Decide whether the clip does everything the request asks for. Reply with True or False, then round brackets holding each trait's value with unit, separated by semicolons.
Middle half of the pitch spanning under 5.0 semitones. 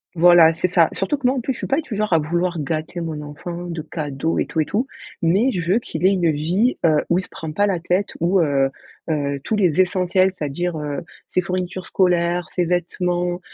True (2.6 semitones)